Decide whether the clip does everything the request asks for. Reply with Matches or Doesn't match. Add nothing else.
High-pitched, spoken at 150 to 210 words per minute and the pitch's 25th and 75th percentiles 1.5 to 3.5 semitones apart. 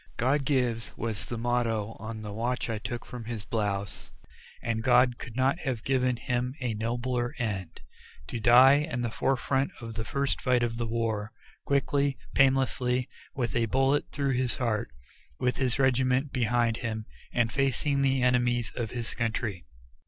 Doesn't match